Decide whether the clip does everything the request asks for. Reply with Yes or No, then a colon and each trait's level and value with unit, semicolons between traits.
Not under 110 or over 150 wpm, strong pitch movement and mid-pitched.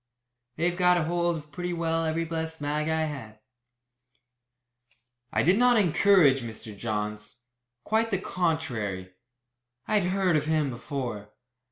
Yes: slow, 135 wpm; wide, 6.2 semitones; medium, 160 Hz